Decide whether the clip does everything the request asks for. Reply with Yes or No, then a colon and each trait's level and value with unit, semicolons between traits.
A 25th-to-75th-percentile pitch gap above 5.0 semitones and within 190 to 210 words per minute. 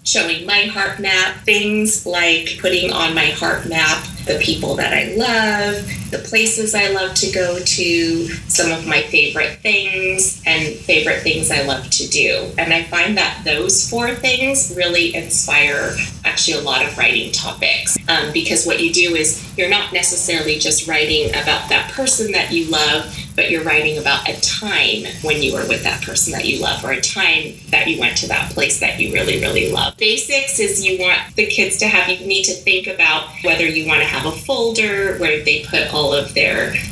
No: average, 4.1 semitones; average, 200 wpm